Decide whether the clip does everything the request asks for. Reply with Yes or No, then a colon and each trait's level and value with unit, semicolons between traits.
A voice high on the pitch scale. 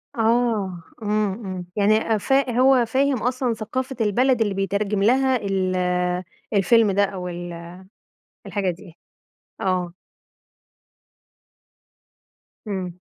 Yes: high, 210 Hz